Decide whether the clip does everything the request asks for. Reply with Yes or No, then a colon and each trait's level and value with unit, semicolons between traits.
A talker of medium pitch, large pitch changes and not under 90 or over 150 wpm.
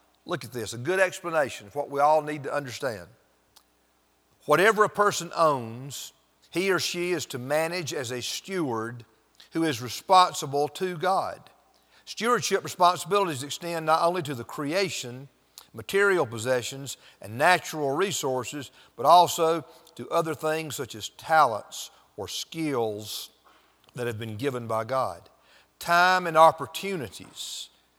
Yes: medium, 150 Hz; wide, 6.0 semitones; slow, 135 wpm